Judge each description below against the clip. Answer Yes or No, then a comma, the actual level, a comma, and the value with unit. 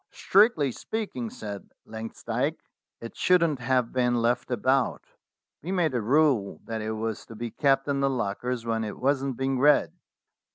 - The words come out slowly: No, average, 160 wpm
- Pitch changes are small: No, average, 3.6 semitones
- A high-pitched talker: No, low, 125 Hz